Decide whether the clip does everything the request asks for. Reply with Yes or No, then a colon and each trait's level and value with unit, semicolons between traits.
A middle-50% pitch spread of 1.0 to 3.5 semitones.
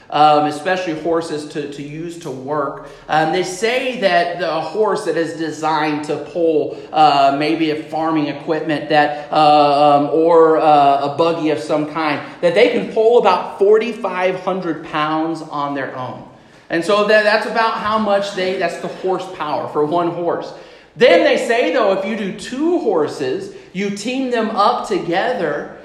No: average, 4.8 semitones